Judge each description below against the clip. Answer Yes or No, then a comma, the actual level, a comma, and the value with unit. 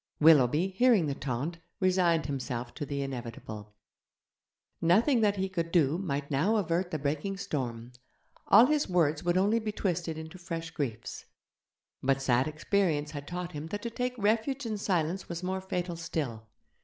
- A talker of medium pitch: Yes, medium, 165 Hz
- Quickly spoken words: No, average, 165 wpm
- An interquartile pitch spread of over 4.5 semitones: Yes, average, 5.2 semitones